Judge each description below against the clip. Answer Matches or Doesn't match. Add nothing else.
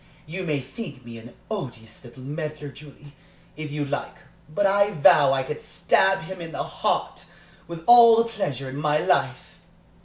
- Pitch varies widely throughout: Matches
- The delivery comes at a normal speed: Matches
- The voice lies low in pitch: Doesn't match